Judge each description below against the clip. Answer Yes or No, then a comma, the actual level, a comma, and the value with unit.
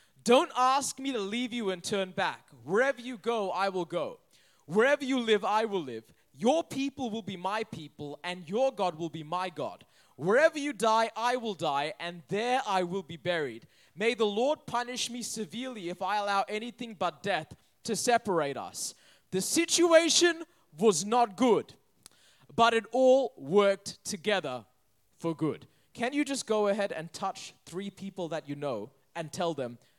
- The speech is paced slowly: No, average, 175 wpm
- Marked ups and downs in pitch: Yes, wide, 5.8 semitones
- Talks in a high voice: Yes, high, 210 Hz